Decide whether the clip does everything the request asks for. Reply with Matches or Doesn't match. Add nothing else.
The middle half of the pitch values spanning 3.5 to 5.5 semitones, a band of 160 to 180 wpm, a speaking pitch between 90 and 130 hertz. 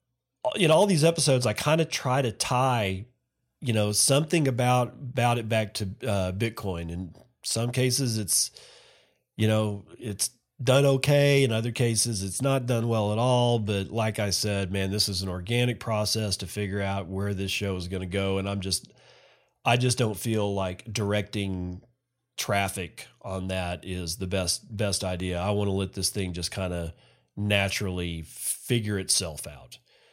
Matches